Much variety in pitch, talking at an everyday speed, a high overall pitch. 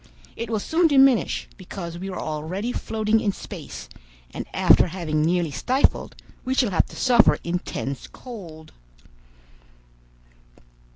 No: wide, 6.0 semitones; slow, 125 wpm; high, 195 Hz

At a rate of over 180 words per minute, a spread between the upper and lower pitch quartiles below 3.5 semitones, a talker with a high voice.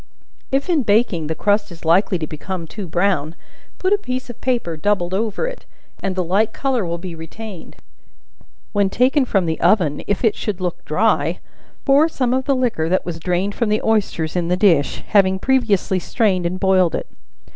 No: average, 190 wpm; average, 4.9 semitones; high, 195 Hz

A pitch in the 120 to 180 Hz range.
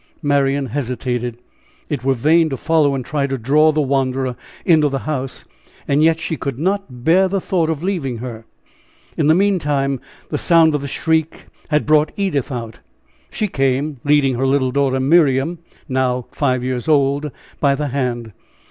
Yes: medium, 140 Hz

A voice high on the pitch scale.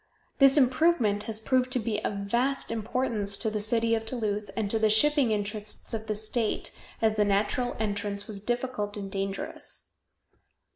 Yes: high, 220 Hz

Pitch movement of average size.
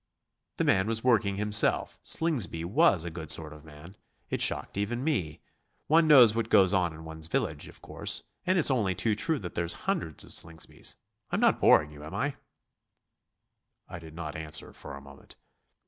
No: wide, 6.2 semitones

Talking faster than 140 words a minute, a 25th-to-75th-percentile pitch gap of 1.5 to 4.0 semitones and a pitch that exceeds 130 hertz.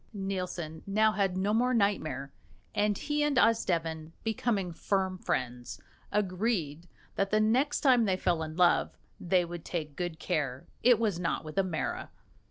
No: average, 160 wpm; average, 4.8 semitones; medium, 185 Hz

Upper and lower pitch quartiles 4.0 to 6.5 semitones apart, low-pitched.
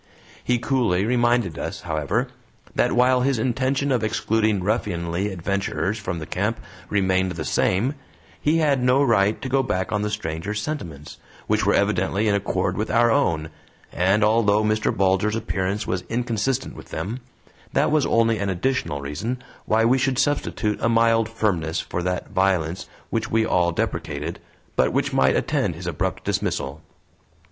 Yes: average, 4.6 semitones; low, 105 Hz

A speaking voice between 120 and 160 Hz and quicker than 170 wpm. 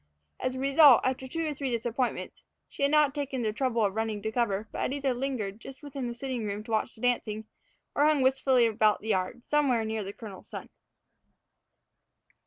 No: high, 245 Hz; average, 200 wpm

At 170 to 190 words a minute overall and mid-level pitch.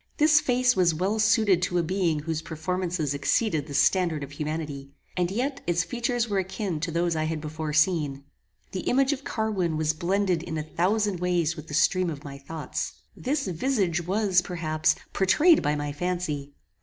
Yes: average, 180 wpm; medium, 175 Hz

